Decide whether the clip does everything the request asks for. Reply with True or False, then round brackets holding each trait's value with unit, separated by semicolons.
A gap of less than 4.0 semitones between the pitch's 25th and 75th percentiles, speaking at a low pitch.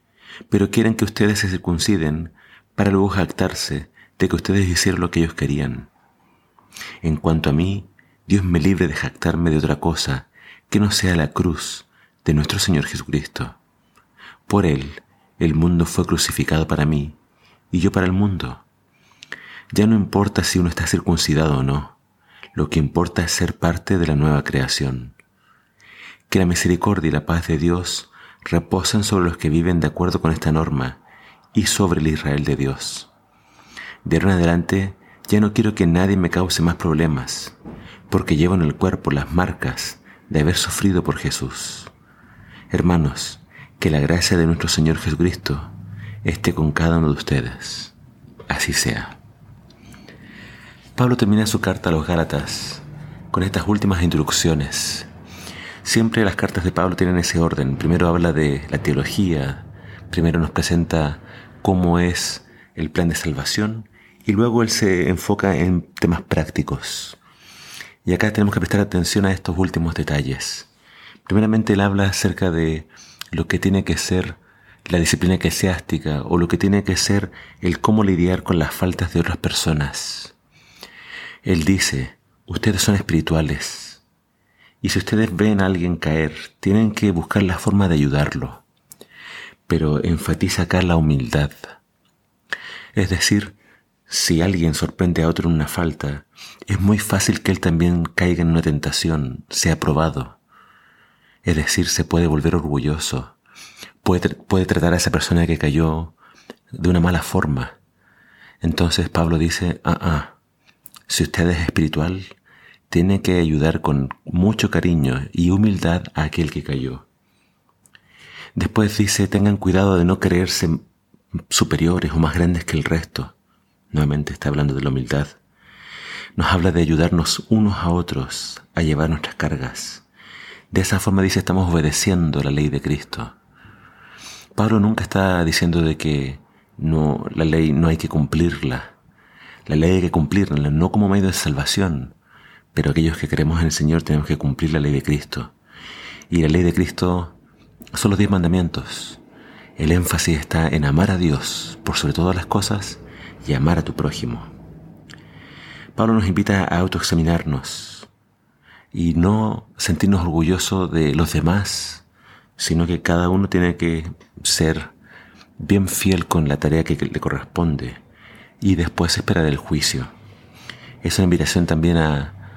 True (3.4 semitones; 85 Hz)